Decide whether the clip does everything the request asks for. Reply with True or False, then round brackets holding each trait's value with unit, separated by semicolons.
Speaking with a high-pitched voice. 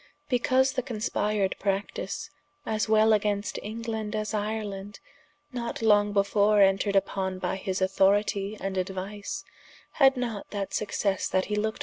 True (210 Hz)